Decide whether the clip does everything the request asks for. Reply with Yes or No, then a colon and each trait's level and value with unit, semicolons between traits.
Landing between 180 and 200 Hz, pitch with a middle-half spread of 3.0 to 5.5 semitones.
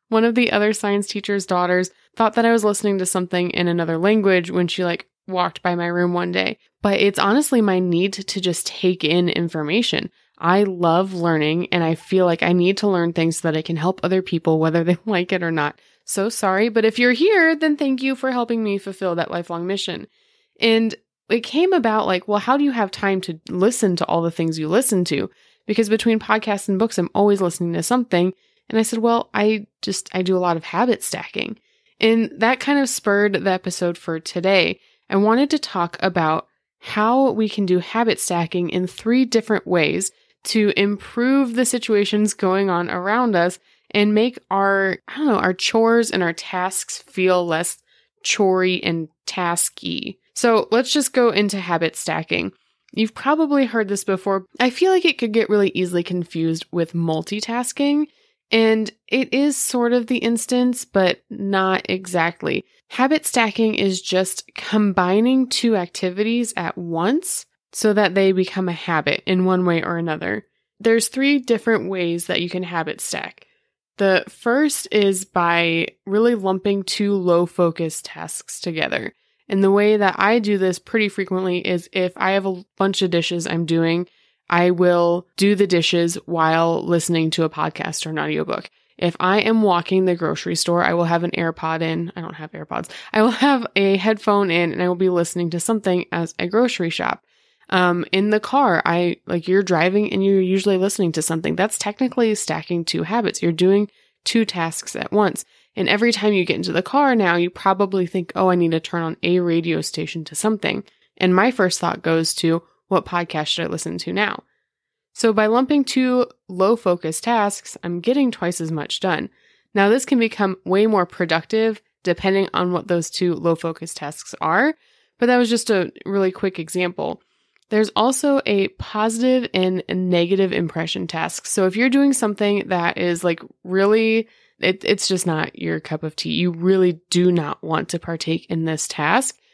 Yes: high, 190 Hz; average, 4.3 semitones